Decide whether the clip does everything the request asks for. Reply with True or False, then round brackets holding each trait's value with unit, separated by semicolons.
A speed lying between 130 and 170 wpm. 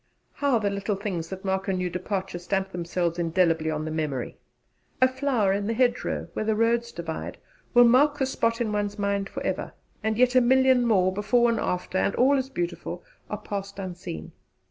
False (195 wpm)